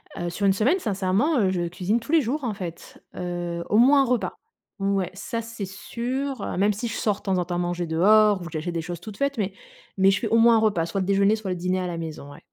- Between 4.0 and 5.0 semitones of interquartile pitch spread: Yes, average, 4.3 semitones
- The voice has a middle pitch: No, high, 195 Hz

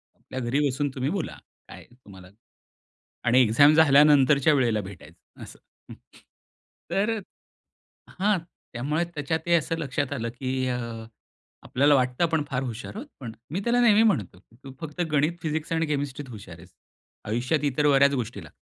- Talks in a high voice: No, medium, 140 Hz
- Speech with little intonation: No, average, 4.2 semitones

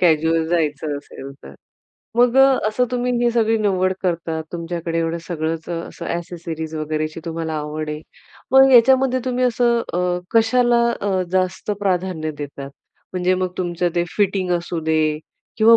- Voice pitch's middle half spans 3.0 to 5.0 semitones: No, wide, 5.6 semitones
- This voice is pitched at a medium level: Yes, medium, 175 Hz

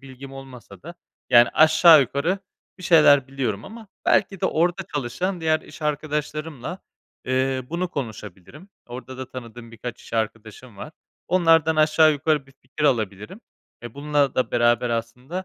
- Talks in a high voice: No, medium, 140 Hz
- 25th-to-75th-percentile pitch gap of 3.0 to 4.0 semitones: No, average, 4.7 semitones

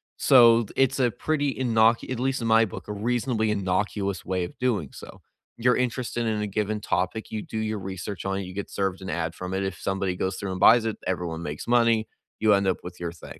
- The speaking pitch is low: Yes, low, 105 Hz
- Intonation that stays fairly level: No, average, 3.6 semitones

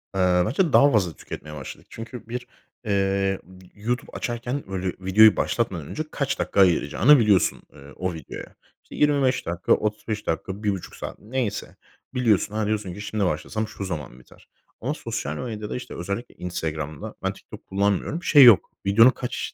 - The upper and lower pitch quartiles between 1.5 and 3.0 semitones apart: No, average, 4.6 semitones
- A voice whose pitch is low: Yes, low, 105 Hz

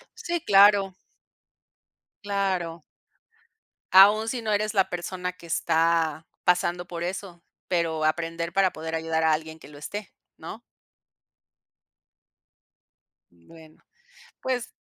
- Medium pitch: Yes, medium, 175 Hz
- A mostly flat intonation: No, average, 3.5 semitones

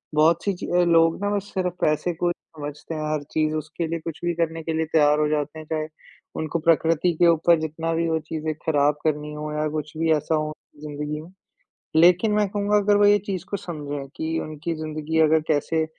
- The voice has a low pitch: No, medium, 160 Hz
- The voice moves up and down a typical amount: No, narrow, 1.9 semitones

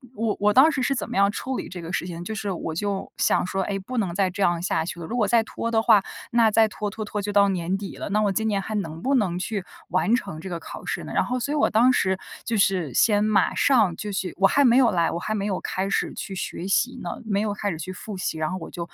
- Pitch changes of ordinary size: Yes, average, 3.4 semitones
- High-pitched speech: Yes, high, 200 Hz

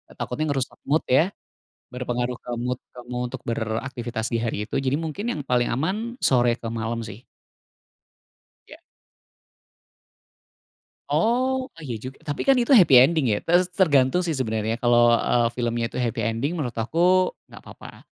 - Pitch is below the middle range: Yes, low, 125 Hz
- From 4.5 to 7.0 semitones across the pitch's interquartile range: Yes, wide, 5.6 semitones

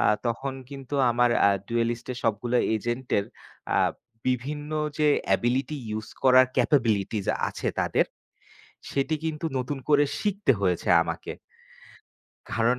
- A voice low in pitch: Yes, low, 125 Hz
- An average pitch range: Yes, average, 3.5 semitones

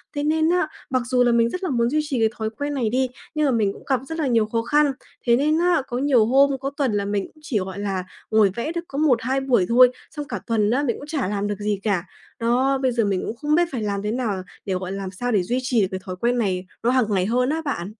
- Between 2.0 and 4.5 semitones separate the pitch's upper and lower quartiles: No, average, 5.1 semitones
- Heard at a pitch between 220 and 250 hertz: Yes, high, 240 Hz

